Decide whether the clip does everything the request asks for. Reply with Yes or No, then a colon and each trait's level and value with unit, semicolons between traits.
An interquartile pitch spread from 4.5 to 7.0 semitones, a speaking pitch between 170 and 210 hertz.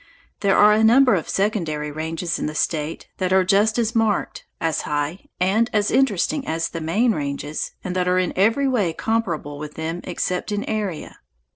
Yes: average, 5.1 semitones; medium, 185 Hz